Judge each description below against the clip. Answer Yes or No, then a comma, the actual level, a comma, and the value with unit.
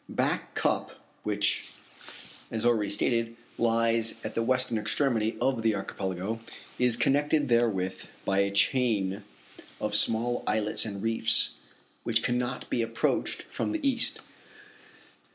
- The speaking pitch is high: No, low, 115 Hz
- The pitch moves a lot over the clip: No, narrow, 2.5 semitones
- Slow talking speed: Yes, slow, 125 wpm